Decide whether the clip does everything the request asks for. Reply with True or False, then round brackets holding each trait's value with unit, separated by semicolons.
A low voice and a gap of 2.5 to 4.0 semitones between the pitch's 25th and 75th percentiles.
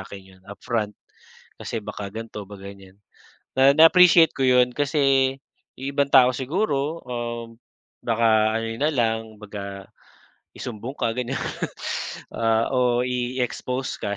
True (120 Hz; 3.5 semitones)